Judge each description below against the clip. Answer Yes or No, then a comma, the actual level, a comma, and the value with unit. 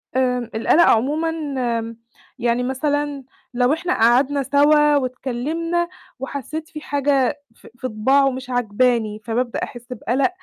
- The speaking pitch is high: Yes, very high, 260 Hz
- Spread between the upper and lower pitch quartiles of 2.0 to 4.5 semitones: Yes, average, 3.2 semitones